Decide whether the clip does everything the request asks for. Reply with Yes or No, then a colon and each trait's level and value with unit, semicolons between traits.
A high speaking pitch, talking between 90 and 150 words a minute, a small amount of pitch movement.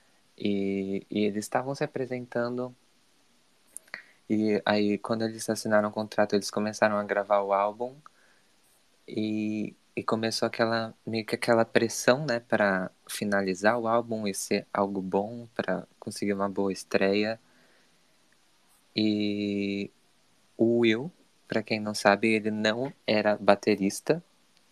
No: low, 105 Hz; average, 125 wpm; narrow, 2.1 semitones